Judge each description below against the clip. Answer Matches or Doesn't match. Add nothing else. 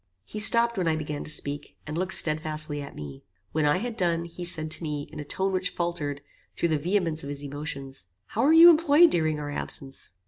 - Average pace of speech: Doesn't match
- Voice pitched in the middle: Matches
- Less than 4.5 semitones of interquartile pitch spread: Matches